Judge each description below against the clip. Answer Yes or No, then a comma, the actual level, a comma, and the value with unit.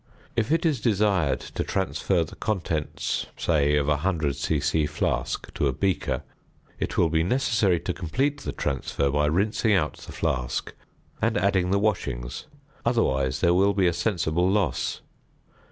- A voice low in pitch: Yes, very low, 85 Hz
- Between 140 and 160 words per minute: Yes, average, 155 wpm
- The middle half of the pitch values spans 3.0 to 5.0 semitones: No, wide, 5.5 semitones